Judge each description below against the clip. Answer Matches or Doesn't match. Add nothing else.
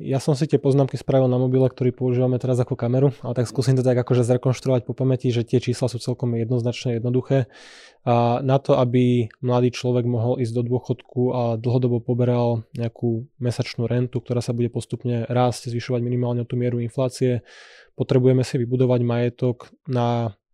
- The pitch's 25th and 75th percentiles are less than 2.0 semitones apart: Matches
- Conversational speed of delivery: Doesn't match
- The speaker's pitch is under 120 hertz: Doesn't match